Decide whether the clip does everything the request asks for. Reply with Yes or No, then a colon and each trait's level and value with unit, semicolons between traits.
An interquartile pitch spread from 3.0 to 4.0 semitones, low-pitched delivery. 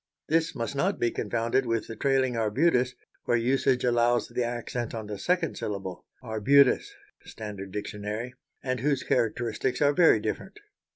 Yes: average, 3.4 semitones; low, 120 Hz